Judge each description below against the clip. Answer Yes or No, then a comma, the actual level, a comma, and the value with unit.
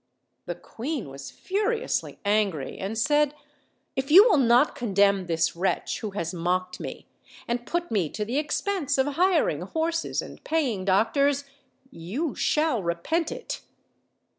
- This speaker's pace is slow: No, average, 150 wpm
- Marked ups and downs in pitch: Yes, wide, 8.5 semitones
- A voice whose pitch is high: Yes, high, 240 Hz